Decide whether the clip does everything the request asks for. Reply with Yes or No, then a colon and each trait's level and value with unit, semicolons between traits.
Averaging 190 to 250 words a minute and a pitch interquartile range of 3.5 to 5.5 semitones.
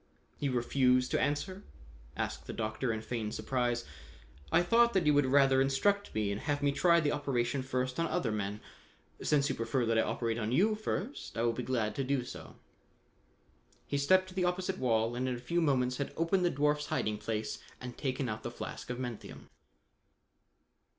Yes: average, 195 wpm; average, 4.1 semitones